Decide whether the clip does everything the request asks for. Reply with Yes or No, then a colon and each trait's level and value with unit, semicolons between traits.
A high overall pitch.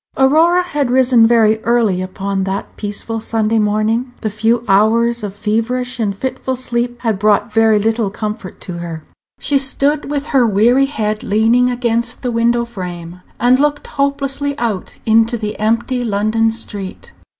Yes: high, 225 Hz